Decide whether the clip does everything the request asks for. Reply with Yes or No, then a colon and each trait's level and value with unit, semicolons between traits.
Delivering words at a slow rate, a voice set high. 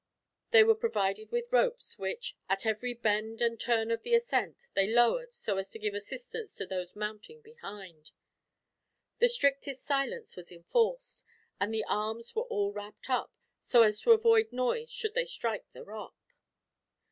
No: average, 165 wpm; high, 235 Hz